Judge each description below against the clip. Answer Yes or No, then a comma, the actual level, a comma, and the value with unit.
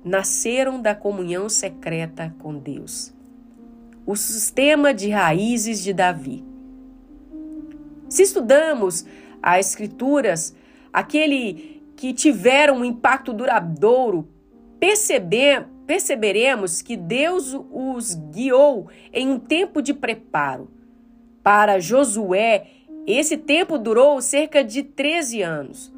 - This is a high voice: Yes, very high, 255 Hz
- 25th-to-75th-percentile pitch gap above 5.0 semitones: Yes, wide, 5.5 semitones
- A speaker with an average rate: No, slow, 95 wpm